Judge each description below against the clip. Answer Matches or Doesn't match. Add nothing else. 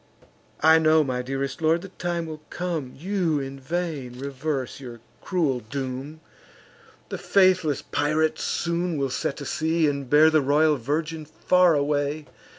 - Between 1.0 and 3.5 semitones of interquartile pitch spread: Matches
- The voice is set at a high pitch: Doesn't match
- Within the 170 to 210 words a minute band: Doesn't match